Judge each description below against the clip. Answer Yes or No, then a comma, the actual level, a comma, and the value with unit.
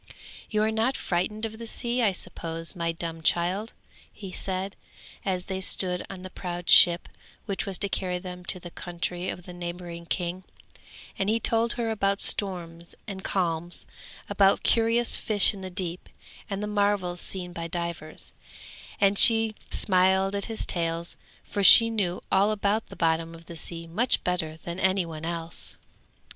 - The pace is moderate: Yes, average, 170 wpm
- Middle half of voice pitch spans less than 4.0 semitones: Yes, average, 2.9 semitones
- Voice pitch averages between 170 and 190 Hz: Yes, medium, 185 Hz